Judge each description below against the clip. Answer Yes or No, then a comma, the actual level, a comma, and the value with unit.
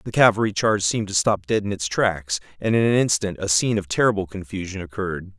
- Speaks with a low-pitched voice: Yes, low, 100 Hz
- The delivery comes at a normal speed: No, fast, 225 wpm